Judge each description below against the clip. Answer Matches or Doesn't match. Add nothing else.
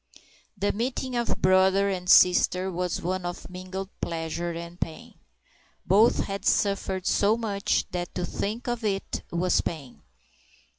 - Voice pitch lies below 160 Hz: Doesn't match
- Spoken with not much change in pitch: Matches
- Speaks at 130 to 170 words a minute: Matches